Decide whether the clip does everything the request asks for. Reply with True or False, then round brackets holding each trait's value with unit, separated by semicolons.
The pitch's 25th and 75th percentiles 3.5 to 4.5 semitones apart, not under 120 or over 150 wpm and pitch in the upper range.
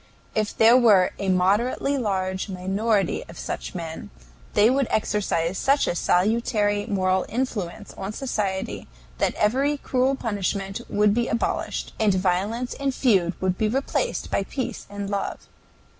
True (3.9 semitones; 145 wpm; 205 Hz)